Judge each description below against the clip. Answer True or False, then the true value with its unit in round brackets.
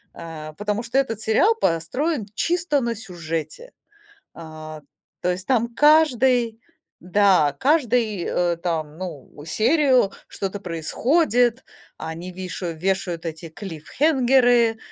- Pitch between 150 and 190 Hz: False (205 Hz)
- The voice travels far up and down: True (7.0 semitones)